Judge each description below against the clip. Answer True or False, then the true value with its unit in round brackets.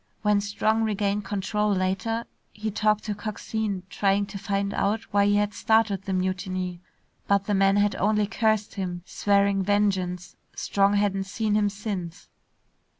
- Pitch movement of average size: False (1.4 semitones)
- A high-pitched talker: True (200 Hz)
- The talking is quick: False (150 wpm)